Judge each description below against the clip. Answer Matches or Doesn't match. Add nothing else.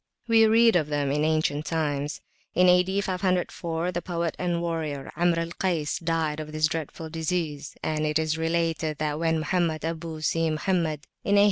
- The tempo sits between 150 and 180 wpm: Matches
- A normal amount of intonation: Doesn't match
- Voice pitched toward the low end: Doesn't match